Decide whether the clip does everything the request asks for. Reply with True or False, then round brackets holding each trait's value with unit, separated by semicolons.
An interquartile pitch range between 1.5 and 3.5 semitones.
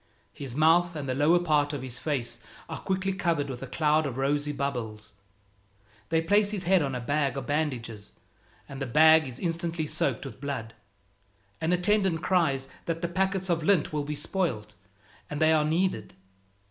False (4.2 semitones)